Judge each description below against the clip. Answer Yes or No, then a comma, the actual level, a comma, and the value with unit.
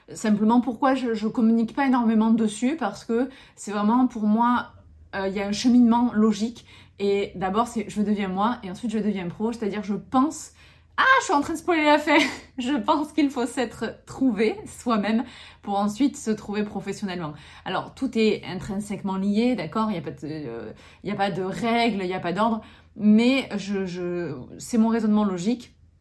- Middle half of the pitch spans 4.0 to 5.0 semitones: No, average, 3.6 semitones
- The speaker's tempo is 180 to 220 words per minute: Yes, average, 190 wpm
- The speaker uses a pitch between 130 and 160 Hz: No, high, 220 Hz